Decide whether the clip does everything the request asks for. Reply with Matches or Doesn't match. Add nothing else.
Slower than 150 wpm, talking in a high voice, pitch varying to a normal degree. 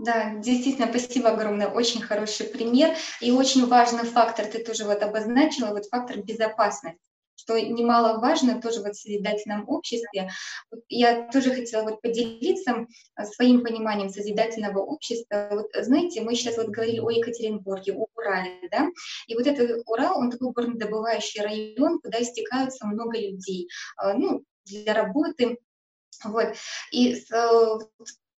Doesn't match